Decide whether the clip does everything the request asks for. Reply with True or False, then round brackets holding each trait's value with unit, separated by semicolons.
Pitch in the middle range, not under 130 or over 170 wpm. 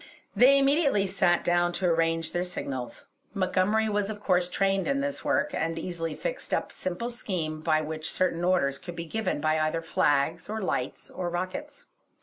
False (180 Hz; 180 wpm)